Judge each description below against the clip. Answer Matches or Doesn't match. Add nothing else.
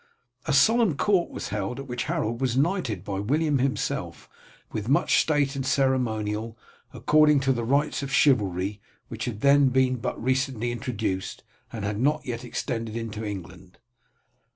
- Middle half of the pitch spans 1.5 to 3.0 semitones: Doesn't match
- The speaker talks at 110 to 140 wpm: Doesn't match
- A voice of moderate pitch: Doesn't match